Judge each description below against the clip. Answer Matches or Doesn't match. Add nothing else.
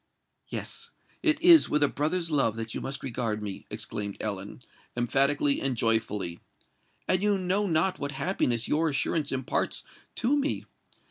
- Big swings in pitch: Matches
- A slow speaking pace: Doesn't match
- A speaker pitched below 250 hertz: Matches